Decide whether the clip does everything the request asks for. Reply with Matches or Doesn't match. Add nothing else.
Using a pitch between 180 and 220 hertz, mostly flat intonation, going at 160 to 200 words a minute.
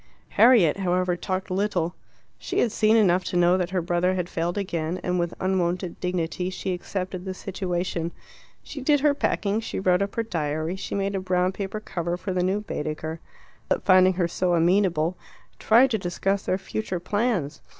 Matches